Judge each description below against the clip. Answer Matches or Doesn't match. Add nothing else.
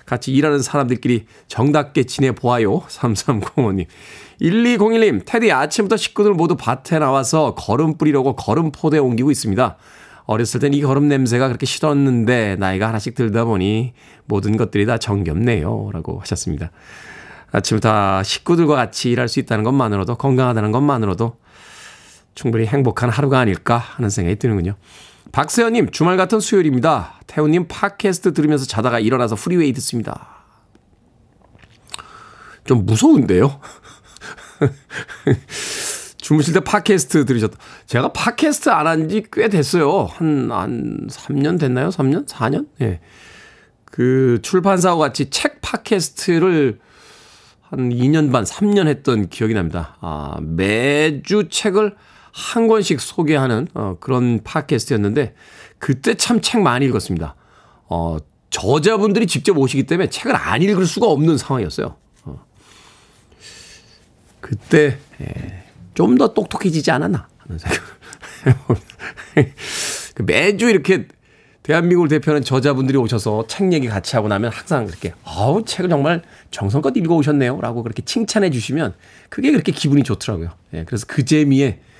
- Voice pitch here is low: Matches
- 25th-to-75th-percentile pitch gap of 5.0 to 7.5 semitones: Matches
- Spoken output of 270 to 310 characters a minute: Matches